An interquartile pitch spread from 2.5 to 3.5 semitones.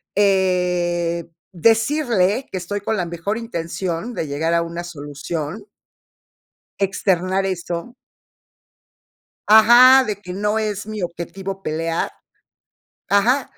No: average, 4.0 semitones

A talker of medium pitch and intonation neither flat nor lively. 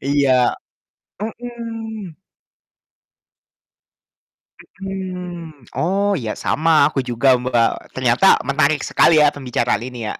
No: medium, 155 Hz; wide, 6.9 semitones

